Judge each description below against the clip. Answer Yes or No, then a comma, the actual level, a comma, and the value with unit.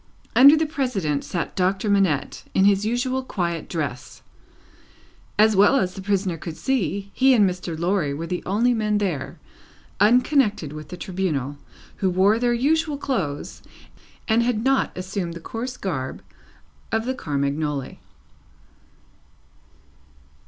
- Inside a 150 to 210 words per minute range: No, slow, 135 wpm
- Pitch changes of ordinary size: No, wide, 6.2 semitones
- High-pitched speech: Yes, high, 195 Hz